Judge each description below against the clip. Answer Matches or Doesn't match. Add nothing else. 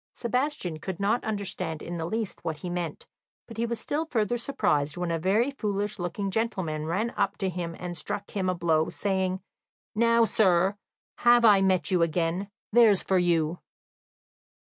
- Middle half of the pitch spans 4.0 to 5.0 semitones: Matches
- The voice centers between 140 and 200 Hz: Matches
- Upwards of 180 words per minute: Doesn't match